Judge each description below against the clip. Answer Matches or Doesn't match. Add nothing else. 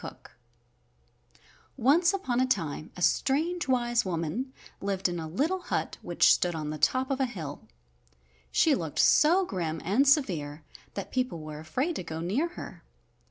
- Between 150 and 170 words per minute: Matches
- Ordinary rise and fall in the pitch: Doesn't match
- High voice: Matches